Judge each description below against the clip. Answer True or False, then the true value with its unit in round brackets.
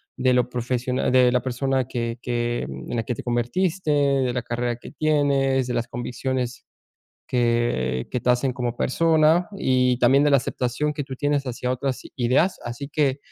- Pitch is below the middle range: True (125 Hz)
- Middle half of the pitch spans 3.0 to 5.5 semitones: False (2.4 semitones)